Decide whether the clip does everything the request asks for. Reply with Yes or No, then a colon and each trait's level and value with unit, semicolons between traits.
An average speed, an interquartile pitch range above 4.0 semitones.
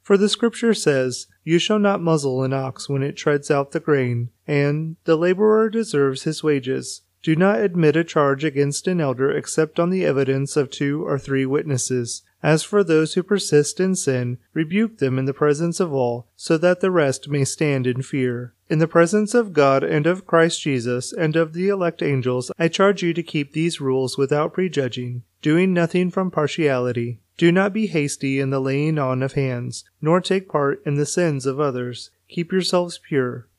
Yes: average, 195 wpm; average, 4.4 semitones